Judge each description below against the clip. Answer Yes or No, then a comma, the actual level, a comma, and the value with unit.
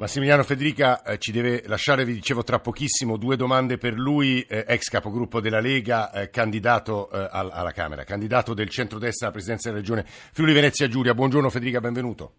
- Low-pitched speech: Yes, low, 120 Hz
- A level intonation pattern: No, average, 3.2 semitones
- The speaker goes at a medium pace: No, fast, 185 wpm